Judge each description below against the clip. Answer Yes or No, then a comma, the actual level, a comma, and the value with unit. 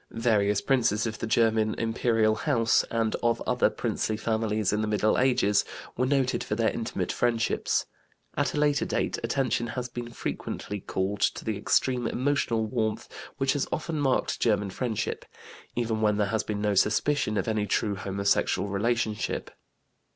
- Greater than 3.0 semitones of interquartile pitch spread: No, narrow, 2.4 semitones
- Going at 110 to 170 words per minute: Yes, average, 160 wpm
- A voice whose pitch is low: Yes, low, 110 Hz